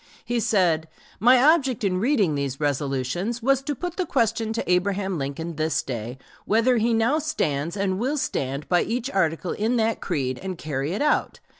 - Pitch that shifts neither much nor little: No, wide, 7.6 semitones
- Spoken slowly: No, average, 180 wpm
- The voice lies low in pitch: No, high, 195 Hz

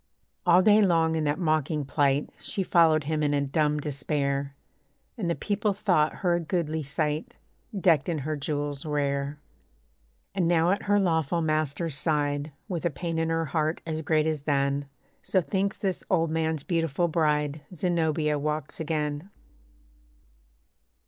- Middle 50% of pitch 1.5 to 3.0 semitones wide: Yes, narrow, 2.5 semitones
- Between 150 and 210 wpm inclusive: Yes, average, 155 wpm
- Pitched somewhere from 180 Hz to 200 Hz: No, medium, 155 Hz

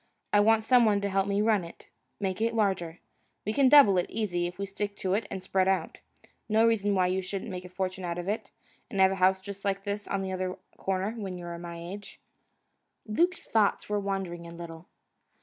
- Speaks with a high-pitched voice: Yes, high, 195 Hz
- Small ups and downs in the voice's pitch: Yes, narrow, 2.2 semitones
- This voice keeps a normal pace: No, fast, 220 wpm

